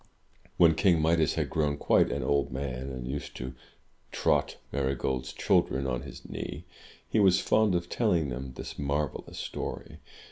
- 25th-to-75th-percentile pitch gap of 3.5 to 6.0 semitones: Yes, average, 3.9 semitones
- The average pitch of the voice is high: No, very low, 70 Hz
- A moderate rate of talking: Yes, average, 155 wpm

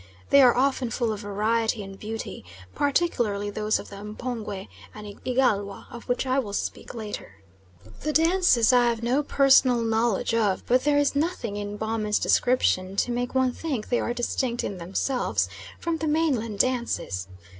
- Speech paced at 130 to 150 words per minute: No, average, 165 wpm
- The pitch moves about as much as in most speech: Yes, average, 3.9 semitones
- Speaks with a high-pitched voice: Yes, high, 235 Hz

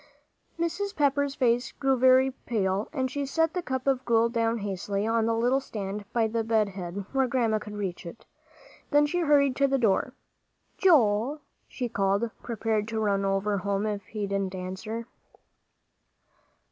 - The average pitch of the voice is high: Yes, high, 230 Hz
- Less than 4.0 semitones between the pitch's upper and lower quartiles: No, average, 4.7 semitones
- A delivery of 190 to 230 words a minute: No, average, 165 wpm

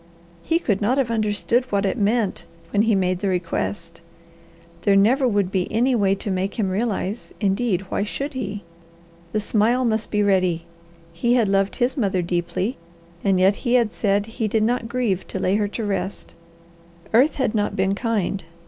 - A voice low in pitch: No, high, 205 Hz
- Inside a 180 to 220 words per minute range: Yes, average, 185 wpm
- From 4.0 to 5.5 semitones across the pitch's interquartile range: No, average, 3.4 semitones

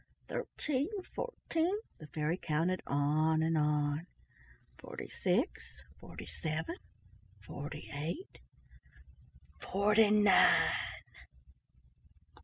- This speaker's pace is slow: Yes, slow, 60 wpm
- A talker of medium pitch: Yes, medium, 160 Hz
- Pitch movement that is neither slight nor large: No, wide, 6.3 semitones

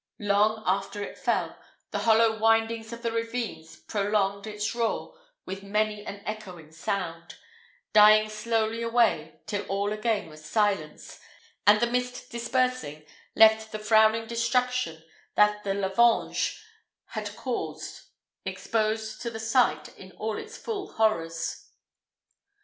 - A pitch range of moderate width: No, narrow, 2.3 semitones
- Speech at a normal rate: No, slow, 125 wpm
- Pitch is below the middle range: No, high, 215 Hz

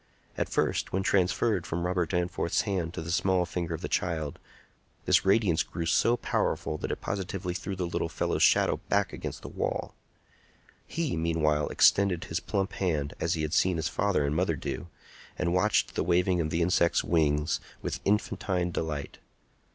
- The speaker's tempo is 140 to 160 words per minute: No, average, 175 wpm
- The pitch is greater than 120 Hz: No, very low, 85 Hz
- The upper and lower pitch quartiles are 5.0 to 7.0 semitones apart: No, average, 2.7 semitones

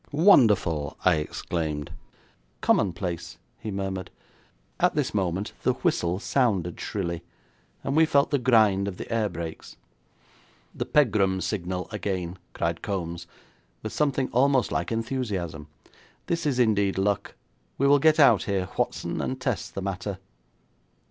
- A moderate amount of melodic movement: No, wide, 6.0 semitones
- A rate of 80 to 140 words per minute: Yes, slow, 135 wpm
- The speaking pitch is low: Yes, low, 100 Hz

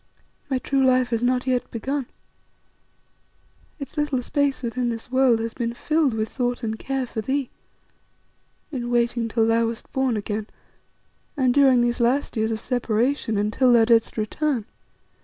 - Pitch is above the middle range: Yes, high, 245 Hz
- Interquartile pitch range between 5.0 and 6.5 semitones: No, narrow, 2.6 semitones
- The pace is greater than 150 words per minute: Yes, average, 160 wpm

